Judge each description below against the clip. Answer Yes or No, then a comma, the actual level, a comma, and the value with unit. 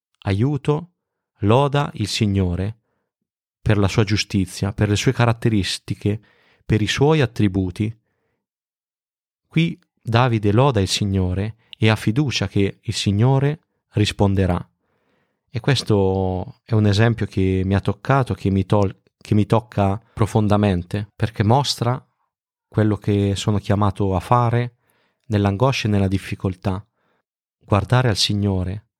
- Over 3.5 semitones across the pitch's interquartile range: No, average, 3.1 semitones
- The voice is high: No, low, 105 Hz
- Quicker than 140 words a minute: No, average, 120 wpm